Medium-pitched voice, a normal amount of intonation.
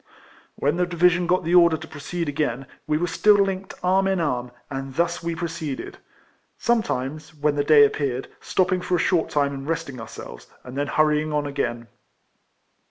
Yes: medium, 155 Hz; average, 3.9 semitones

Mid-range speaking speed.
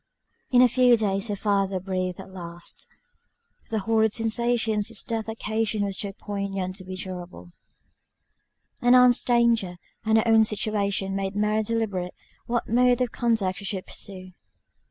Yes: average, 155 wpm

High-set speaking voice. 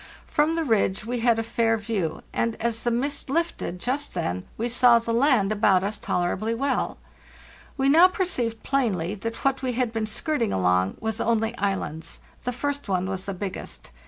Yes: high, 230 Hz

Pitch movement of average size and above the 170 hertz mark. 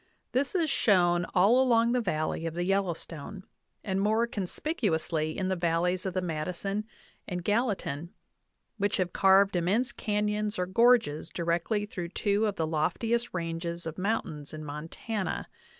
Yes: average, 4.0 semitones; medium, 185 Hz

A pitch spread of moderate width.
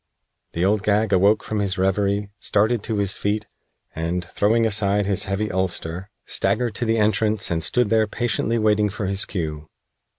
No: narrow, 2.3 semitones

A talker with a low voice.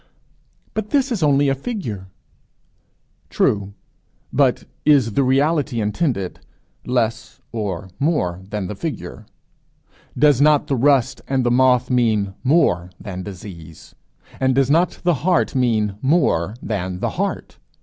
Yes: low, 125 Hz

